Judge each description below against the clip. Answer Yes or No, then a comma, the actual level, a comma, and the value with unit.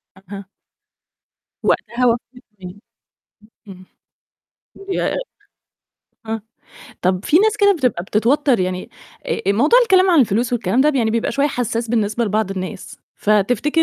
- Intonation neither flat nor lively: No, wide, 6.3 semitones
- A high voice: Yes, high, 230 Hz